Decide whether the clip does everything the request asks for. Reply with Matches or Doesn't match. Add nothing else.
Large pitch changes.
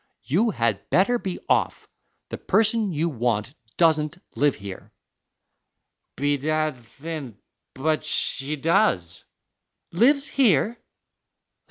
Matches